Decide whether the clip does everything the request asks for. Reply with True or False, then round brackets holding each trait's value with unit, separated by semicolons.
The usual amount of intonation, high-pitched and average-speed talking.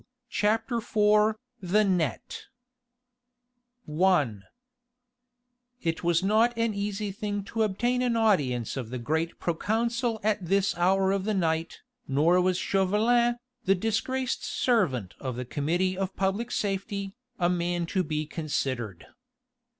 False (4.6 semitones; 195 Hz; 125 wpm)